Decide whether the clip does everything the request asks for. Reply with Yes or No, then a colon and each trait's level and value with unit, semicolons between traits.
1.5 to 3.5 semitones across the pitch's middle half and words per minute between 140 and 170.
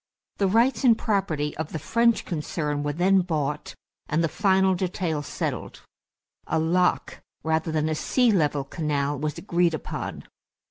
No: average, 4.1 semitones; average, 150 wpm